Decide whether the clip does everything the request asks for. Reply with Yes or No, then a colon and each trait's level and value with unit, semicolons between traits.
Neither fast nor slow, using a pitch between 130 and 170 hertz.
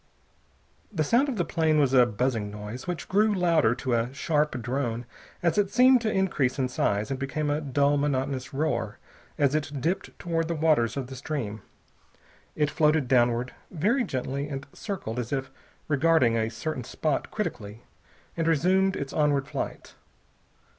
Yes: average, 165 wpm; medium, 140 Hz